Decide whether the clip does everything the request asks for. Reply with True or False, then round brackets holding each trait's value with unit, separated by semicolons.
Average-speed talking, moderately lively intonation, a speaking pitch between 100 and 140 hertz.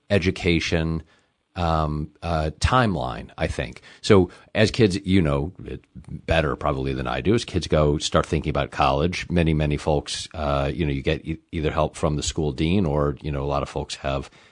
False (190 wpm; 3.2 semitones; 80 Hz)